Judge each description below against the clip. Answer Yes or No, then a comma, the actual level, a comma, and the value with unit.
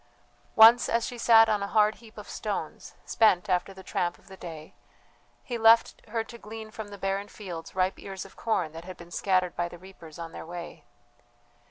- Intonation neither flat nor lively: Yes, average, 3.9 semitones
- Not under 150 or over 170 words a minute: No, fast, 205 wpm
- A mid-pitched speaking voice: No, high, 195 Hz